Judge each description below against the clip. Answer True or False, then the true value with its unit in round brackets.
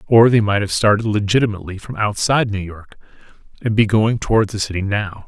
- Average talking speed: True (195 wpm)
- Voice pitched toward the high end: False (105 Hz)